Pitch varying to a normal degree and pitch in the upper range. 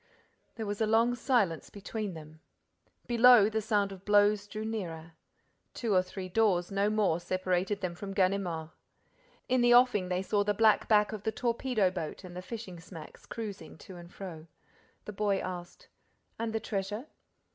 Yes: average, 3.1 semitones; high, 200 Hz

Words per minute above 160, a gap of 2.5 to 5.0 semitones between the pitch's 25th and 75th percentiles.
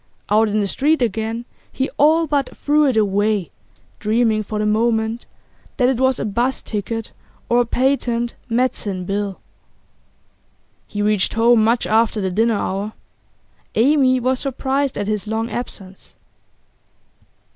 No: average, 140 wpm; average, 3.3 semitones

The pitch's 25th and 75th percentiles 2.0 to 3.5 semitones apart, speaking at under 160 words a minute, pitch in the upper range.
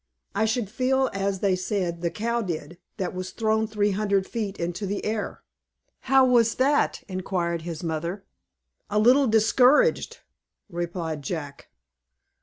No: average, 4.3 semitones; average, 140 wpm; high, 200 Hz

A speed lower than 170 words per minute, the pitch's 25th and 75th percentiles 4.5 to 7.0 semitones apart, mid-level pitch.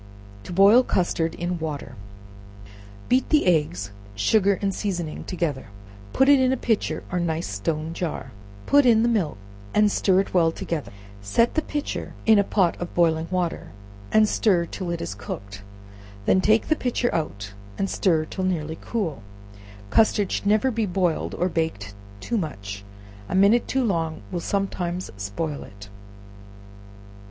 Yes: average, 160 wpm; average, 5.0 semitones; medium, 175 Hz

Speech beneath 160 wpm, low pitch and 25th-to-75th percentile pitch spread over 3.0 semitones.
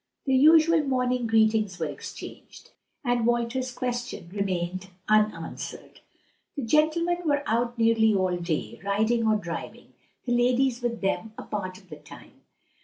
No: average, 140 wpm; high, 230 Hz; average, 4.1 semitones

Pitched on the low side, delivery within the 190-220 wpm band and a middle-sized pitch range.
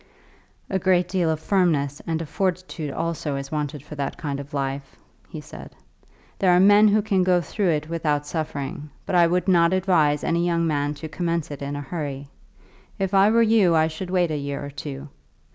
No: medium, 160 Hz; fast, 205 wpm; average, 4.0 semitones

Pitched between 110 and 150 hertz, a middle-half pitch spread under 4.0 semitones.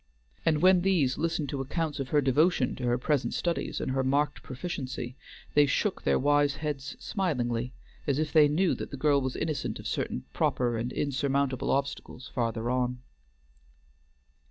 Yes: medium, 140 Hz; average, 3.0 semitones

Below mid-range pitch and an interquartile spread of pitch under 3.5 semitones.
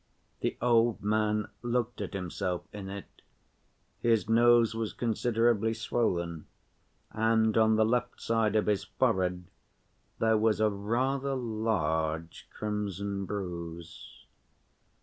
Yes: low, 110 Hz; average, 2.7 semitones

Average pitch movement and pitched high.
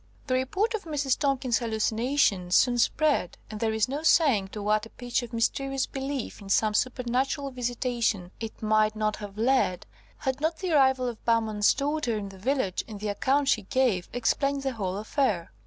Yes: average, 4.2 semitones; high, 240 Hz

